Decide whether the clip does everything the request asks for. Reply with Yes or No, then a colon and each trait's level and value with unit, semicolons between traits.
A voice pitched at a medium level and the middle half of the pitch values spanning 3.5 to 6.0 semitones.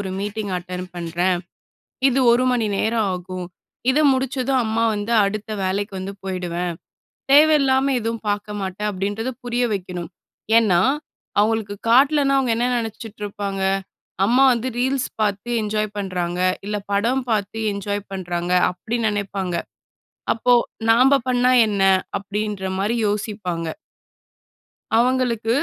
No: high, 210 Hz; average, 3.9 semitones